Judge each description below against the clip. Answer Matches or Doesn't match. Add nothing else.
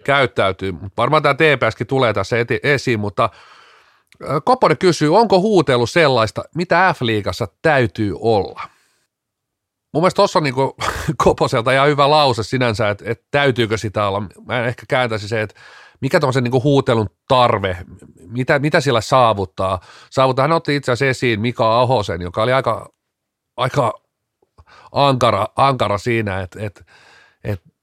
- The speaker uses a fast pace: Doesn't match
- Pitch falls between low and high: Doesn't match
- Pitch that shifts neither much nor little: Matches